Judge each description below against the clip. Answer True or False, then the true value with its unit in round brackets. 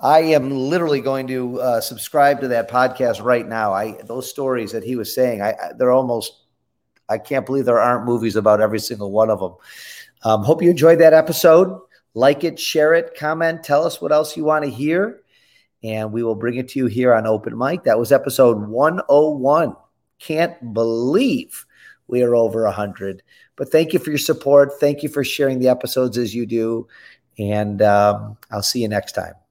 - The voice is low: True (125 Hz)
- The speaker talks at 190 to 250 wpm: True (195 wpm)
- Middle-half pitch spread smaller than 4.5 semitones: False (4.8 semitones)